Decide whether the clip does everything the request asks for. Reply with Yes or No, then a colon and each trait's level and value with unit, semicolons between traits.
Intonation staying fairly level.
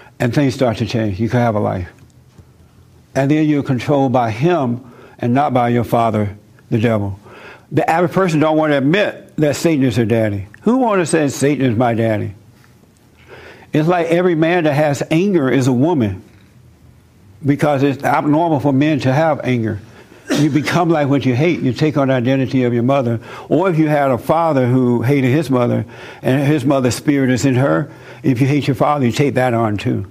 No: average, 3.9 semitones